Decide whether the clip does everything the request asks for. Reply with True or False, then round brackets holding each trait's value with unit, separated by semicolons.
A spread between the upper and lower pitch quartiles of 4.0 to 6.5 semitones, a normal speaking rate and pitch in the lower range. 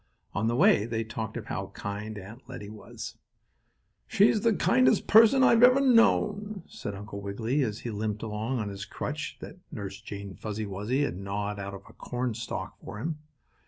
True (5.4 semitones; 185 wpm; 110 Hz)